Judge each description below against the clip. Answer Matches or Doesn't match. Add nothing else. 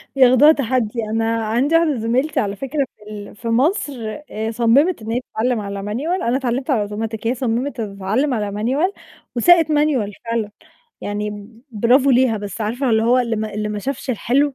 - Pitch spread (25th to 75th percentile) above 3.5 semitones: Matches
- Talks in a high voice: Matches